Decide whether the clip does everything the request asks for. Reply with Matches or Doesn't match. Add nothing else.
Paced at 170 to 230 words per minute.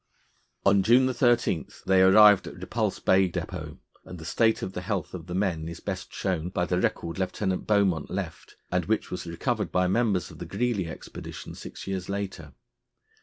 Matches